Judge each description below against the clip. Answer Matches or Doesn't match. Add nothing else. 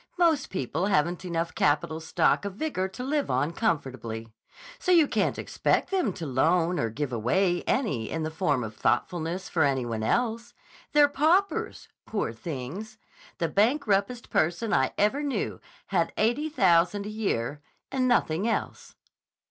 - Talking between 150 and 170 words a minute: Matches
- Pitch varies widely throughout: Matches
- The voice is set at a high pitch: Doesn't match